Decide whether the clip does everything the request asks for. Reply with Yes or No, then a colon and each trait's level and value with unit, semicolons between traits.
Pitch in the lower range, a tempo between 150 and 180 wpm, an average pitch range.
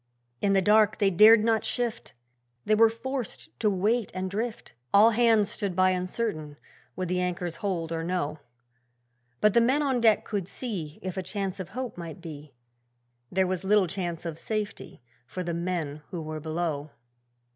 No: high, 190 Hz; average, 175 wpm; average, 4.1 semitones